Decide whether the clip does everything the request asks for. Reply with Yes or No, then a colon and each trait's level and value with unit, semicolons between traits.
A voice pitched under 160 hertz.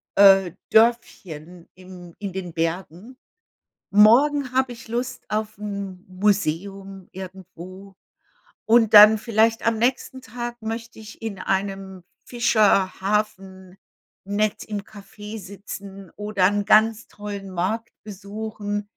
No: high, 205 Hz